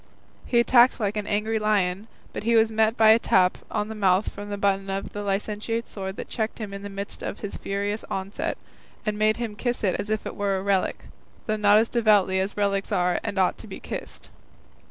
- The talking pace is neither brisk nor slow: No, fast, 225 wpm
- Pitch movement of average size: No, narrow, 1.8 semitones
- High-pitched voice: Yes, high, 205 Hz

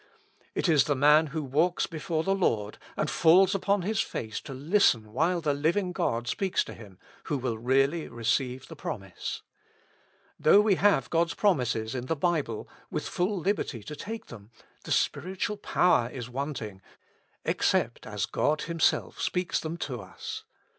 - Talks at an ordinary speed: Yes, average, 160 wpm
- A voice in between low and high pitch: Yes, medium, 150 Hz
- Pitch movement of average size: No, wide, 6.6 semitones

